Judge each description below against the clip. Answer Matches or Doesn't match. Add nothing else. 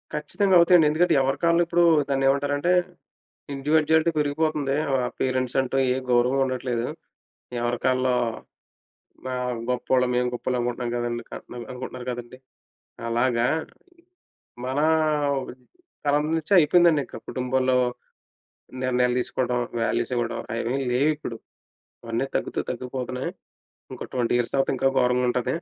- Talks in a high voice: Doesn't match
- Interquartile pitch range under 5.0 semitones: Matches